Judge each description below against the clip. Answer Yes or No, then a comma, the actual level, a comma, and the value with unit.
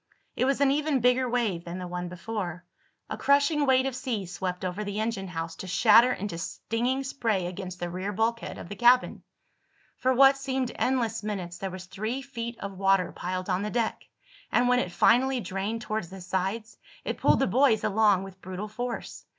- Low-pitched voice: No, high, 215 Hz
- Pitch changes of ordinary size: Yes, average, 5.0 semitones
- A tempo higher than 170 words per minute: Yes, average, 195 wpm